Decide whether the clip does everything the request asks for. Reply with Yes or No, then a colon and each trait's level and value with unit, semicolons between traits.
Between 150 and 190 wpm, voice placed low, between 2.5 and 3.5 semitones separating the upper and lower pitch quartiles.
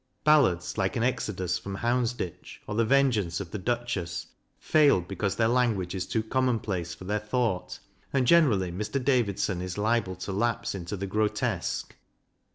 No: average, 165 wpm; low, 105 Hz; average, 4.6 semitones